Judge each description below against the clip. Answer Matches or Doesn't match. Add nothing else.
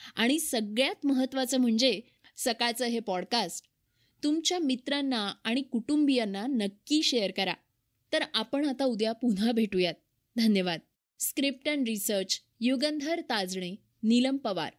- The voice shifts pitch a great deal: Doesn't match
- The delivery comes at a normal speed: Matches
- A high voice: Matches